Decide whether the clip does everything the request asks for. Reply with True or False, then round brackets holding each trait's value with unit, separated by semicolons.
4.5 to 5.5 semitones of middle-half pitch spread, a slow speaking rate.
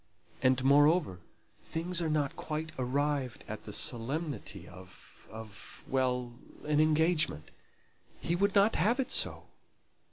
True (4.8 semitones; 125 wpm)